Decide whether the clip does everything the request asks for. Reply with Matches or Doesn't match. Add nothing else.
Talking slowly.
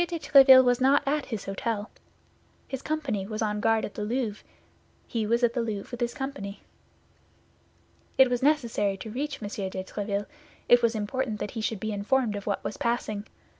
Doesn't match